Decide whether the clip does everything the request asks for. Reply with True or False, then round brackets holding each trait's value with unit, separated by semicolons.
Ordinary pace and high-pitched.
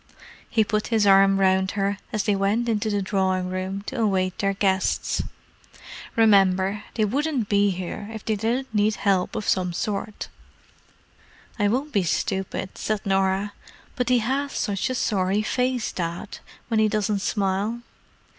True (155 wpm; 205 Hz)